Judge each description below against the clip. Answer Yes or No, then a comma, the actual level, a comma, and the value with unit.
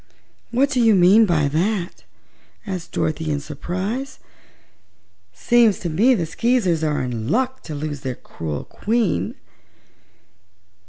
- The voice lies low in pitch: No, medium, 180 Hz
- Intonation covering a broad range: Yes, wide, 7.1 semitones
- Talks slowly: Yes, slow, 125 wpm